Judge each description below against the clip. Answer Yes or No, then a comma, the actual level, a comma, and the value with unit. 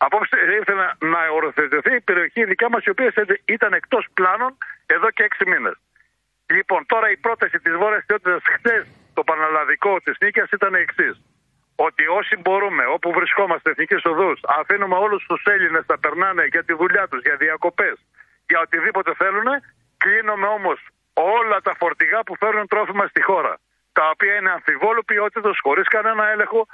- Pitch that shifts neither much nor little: Yes, average, 4.2 semitones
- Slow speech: No, average, 160 wpm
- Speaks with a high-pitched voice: Yes, high, 200 Hz